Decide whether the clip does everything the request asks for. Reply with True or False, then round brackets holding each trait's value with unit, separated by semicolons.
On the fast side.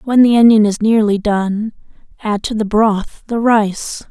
False (175 wpm)